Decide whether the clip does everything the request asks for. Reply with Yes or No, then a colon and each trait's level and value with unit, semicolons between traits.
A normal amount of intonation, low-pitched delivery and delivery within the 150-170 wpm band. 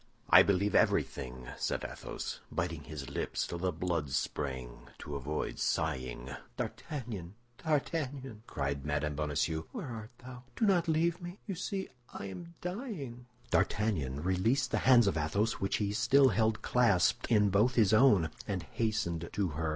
No: wide, 8.6 semitones; low, 100 Hz; average, 155 wpm